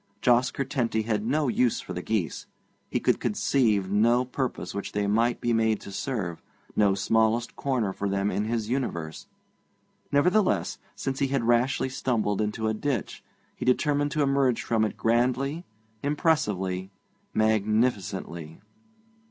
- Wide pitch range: No, average, 4.2 semitones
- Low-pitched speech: Yes, low, 115 Hz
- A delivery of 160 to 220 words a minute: No, average, 145 wpm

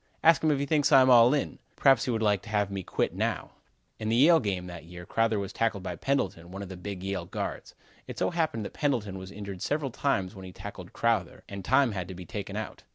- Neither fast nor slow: No, fast, 250 wpm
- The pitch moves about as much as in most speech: No, wide, 5.7 semitones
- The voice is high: No, low, 105 Hz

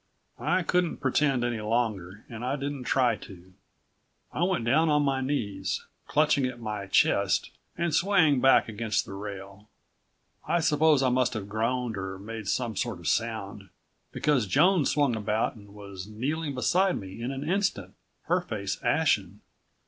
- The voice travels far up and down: Yes, wide, 6.1 semitones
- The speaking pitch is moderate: No, low, 120 Hz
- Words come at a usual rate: Yes, average, 160 wpm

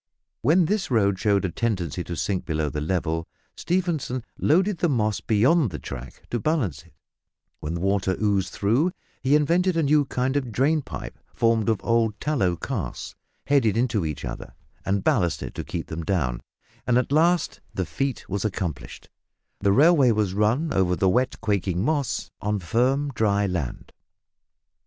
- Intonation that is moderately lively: No, wide, 7.0 semitones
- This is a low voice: Yes, low, 110 Hz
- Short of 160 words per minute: No, average, 165 wpm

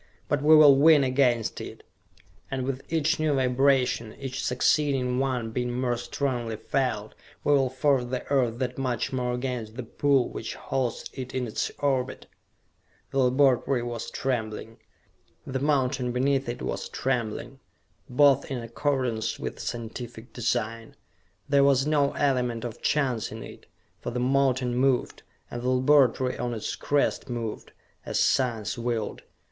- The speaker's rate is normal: Yes, average, 150 wpm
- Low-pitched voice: Yes, low, 125 Hz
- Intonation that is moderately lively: No, narrow, 2.2 semitones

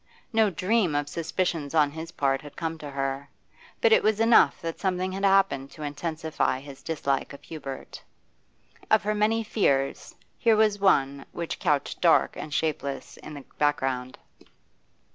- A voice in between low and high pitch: Yes, medium, 160 Hz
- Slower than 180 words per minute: Yes, average, 160 wpm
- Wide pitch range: Yes, wide, 5.7 semitones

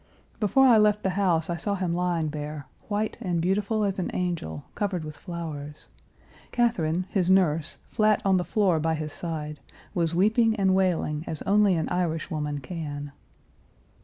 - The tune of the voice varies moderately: Yes, average, 4.1 semitones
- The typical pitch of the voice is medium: Yes, medium, 175 Hz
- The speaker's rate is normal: Yes, average, 160 wpm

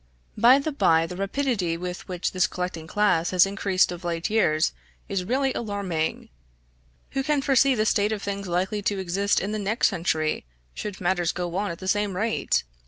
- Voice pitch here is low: No, high, 195 Hz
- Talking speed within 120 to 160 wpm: No, average, 185 wpm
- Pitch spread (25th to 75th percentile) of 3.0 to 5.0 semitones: Yes, average, 3.3 semitones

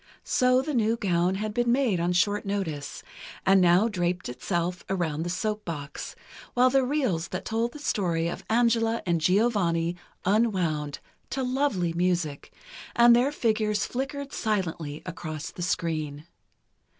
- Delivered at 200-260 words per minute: No, average, 145 wpm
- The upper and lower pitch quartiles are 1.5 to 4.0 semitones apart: No, wide, 5.5 semitones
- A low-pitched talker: No, high, 190 Hz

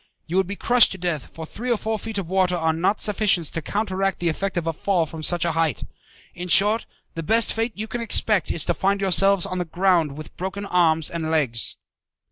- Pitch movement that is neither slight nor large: Yes, average, 3.5 semitones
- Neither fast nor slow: No, fast, 230 wpm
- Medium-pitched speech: Yes, medium, 180 Hz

